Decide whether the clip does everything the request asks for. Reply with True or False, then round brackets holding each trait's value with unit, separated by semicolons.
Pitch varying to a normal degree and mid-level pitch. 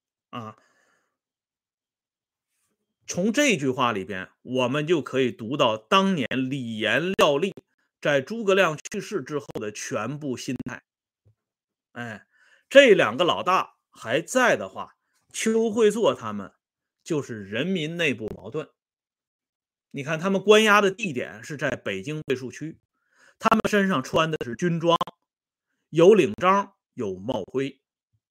False (7.9 semitones; 155 Hz)